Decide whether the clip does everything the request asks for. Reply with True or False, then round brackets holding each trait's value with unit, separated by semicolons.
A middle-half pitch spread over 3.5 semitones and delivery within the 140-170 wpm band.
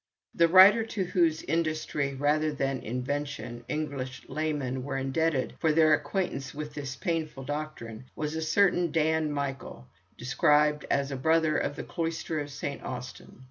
False (2.9 semitones; 150 wpm)